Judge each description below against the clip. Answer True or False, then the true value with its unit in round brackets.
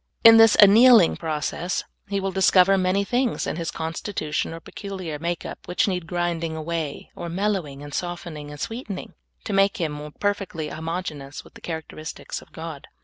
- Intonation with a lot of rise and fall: False (3.7 semitones)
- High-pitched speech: False (175 Hz)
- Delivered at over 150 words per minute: True (160 wpm)